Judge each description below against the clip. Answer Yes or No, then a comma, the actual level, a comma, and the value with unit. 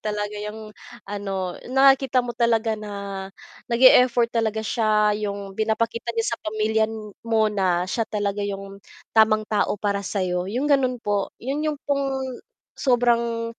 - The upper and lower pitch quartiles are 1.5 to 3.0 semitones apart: Yes, narrow, 2.6 semitones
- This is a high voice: Yes, high, 220 Hz